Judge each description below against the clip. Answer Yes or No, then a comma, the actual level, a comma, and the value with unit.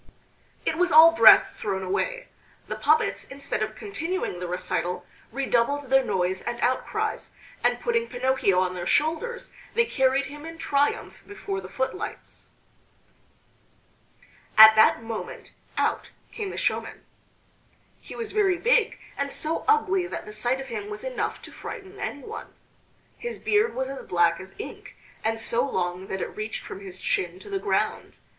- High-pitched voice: Yes, very high, 270 Hz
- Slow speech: No, average, 160 wpm